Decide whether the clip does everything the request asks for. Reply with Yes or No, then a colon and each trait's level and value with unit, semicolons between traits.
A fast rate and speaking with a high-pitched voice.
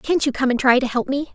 Yes: fast, 355 wpm; very high, 265 Hz